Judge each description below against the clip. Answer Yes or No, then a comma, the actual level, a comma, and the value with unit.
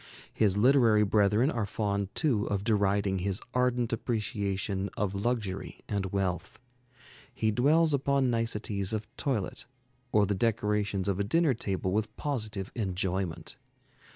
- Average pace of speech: No, slow, 130 wpm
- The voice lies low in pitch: Yes, low, 105 Hz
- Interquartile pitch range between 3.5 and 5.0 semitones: No, average, 3.1 semitones